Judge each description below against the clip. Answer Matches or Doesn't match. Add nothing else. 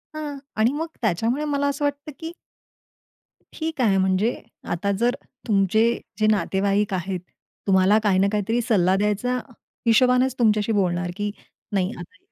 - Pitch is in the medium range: Doesn't match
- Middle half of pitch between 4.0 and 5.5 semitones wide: Matches